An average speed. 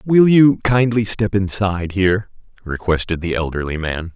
Yes: average, 145 wpm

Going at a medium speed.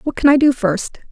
No: fast, 270 wpm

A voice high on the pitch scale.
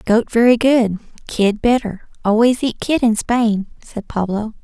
Yes: high, 225 Hz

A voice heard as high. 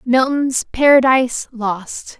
Yes: very high, 250 Hz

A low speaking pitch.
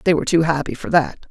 No: medium, 155 Hz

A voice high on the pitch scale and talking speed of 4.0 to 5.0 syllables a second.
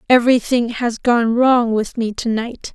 Yes: high, 235 Hz; 4.3 syllables/s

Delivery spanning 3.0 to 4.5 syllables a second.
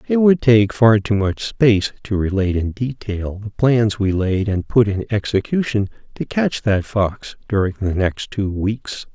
Yes: 4.3 syllables/s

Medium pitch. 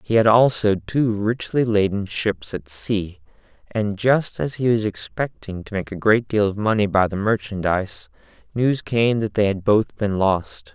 No: low, 105 Hz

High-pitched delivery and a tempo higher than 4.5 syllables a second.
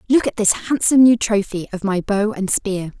Yes: high, 210 Hz; 5.2 syllables/s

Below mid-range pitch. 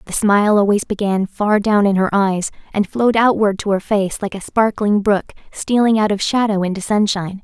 No: high, 205 Hz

